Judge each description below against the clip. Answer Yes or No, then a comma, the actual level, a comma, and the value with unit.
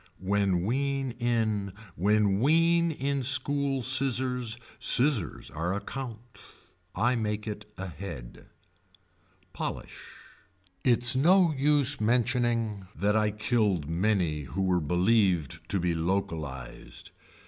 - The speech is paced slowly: Yes, slow, 105 wpm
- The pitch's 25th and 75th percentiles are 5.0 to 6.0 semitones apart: Yes, wide, 5.5 semitones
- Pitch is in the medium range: No, low, 110 Hz